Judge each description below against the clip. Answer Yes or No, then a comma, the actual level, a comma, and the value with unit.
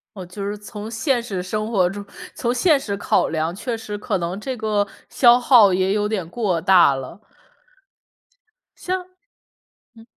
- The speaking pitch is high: Yes, high, 205 Hz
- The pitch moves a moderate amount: Yes, average, 3.7 semitones